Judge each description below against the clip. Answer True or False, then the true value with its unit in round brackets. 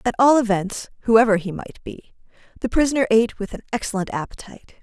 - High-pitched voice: True (220 Hz)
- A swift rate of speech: False (175 wpm)